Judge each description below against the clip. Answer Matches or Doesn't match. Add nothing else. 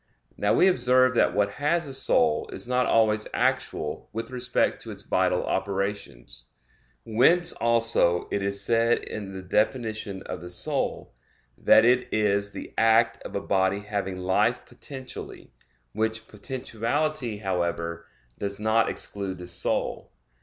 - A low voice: Matches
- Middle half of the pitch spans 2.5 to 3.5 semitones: Doesn't match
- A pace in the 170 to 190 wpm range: Doesn't match